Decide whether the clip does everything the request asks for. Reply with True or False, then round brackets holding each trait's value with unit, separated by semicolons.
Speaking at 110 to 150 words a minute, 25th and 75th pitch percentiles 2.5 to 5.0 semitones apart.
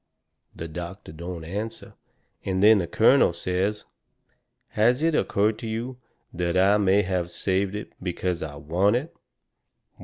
True (145 wpm; 3.6 semitones)